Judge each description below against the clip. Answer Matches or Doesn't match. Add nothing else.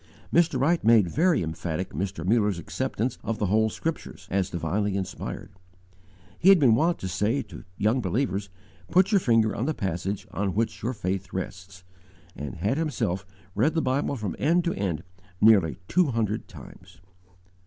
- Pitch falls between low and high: Doesn't match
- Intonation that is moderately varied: Doesn't match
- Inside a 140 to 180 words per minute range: Matches